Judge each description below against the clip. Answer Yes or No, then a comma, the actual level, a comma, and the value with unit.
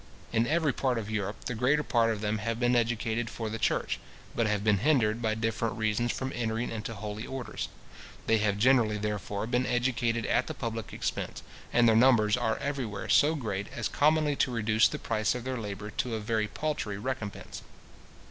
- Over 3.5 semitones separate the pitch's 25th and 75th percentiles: No, narrow, 2.5 semitones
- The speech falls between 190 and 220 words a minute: Yes, average, 195 wpm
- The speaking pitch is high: No, low, 115 Hz